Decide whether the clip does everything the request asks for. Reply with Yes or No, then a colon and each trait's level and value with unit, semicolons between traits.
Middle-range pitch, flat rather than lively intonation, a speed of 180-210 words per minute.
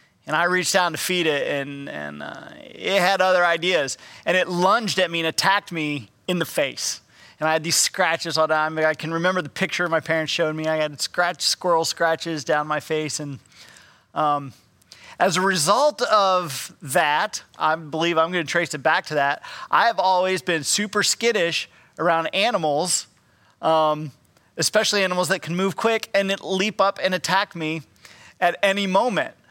No: medium, 170 Hz; average, 3.2 semitones; average, 190 wpm